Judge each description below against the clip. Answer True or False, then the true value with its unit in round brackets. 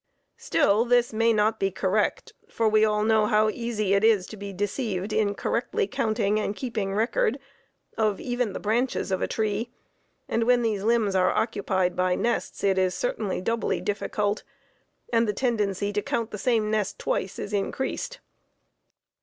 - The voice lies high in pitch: True (215 Hz)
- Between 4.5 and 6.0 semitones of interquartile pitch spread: False (2.4 semitones)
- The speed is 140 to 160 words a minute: False (170 wpm)